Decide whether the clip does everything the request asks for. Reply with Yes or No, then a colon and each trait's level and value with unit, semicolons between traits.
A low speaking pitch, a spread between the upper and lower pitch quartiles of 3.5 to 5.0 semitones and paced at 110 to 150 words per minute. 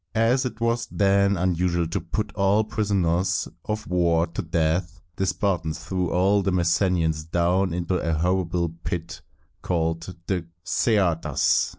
No: very low, 90 Hz; average, 2.8 semitones; average, 145 wpm